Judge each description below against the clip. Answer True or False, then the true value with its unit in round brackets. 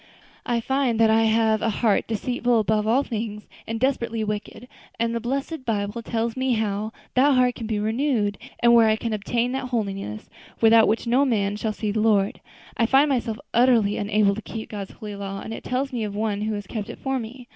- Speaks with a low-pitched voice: False (225 Hz)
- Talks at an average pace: False (215 wpm)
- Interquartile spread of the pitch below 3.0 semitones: True (2.5 semitones)